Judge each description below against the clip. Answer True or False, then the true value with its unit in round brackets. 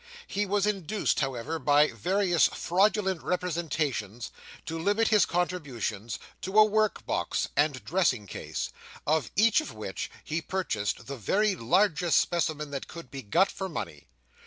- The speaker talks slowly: False (145 wpm)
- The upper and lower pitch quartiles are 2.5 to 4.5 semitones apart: False (5.6 semitones)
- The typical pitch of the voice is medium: True (170 Hz)